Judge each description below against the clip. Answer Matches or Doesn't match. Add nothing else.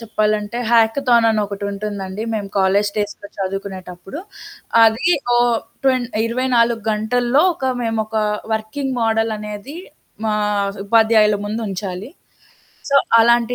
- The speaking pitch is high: Matches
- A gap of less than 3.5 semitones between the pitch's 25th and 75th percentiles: Matches